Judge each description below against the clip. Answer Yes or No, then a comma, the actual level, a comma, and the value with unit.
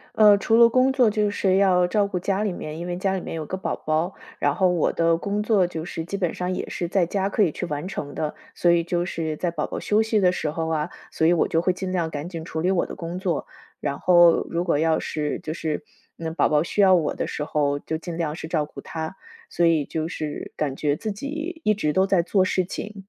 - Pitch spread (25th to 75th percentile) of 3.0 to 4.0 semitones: Yes, average, 3.4 semitones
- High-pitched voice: No, medium, 175 Hz